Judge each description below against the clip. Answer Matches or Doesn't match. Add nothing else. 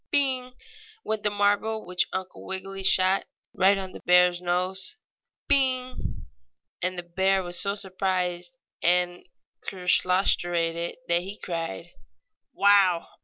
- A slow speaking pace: Matches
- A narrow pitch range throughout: Matches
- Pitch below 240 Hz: Matches